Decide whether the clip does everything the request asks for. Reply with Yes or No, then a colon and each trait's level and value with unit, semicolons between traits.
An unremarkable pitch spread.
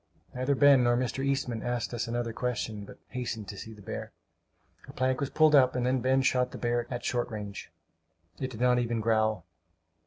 No: narrow, 2.1 semitones